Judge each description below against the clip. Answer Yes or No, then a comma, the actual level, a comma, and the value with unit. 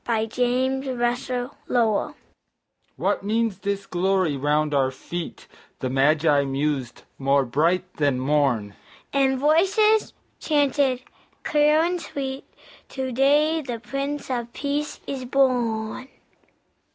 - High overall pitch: Yes, high, 235 Hz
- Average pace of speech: No, slow, 110 wpm